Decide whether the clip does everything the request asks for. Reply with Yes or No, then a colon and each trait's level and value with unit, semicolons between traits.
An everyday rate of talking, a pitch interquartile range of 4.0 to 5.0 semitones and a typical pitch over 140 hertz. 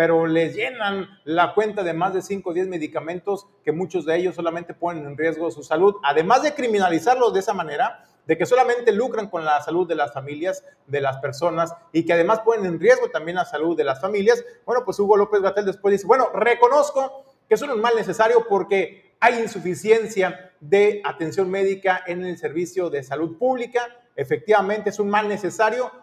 No: fast, 200 wpm; average, 4.7 semitones; high, 190 Hz